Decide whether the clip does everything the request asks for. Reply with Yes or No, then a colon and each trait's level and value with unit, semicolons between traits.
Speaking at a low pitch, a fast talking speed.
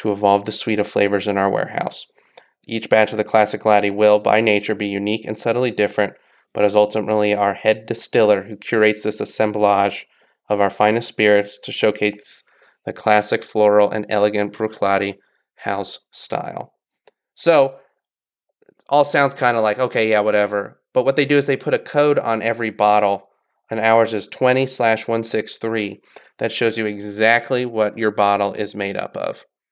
No: low, 105 Hz; average, 170 wpm